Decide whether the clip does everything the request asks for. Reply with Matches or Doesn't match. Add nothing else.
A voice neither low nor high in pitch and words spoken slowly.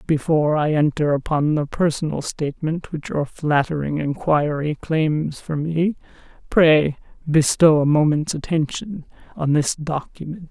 Matches